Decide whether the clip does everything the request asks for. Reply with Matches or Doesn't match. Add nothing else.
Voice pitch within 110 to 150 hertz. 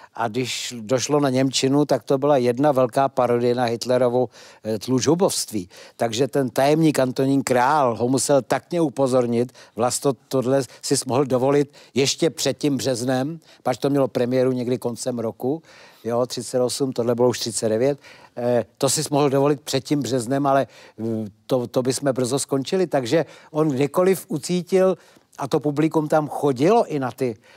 Matches